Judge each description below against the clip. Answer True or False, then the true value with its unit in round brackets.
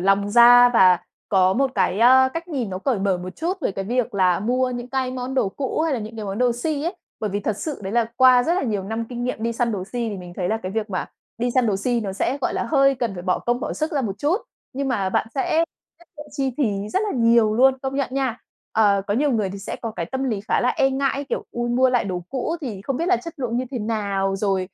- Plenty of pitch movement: False (4.8 semitones)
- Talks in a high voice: True (240 Hz)